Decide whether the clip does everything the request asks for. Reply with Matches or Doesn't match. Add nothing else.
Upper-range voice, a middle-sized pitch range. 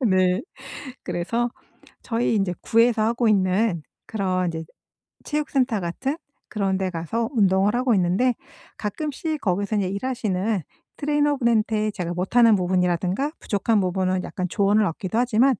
Matches